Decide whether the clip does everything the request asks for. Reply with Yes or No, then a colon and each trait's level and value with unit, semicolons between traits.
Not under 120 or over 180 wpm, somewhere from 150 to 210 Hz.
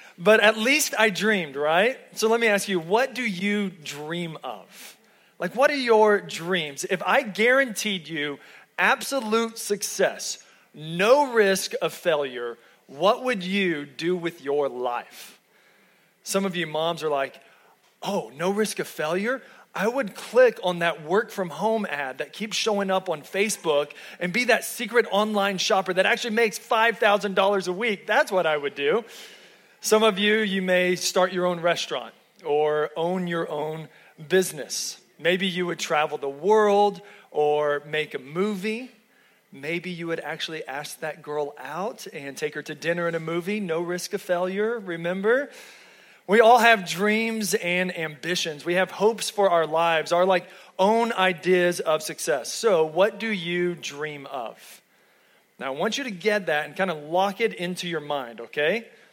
Yes: average, 170 wpm; medium, 185 Hz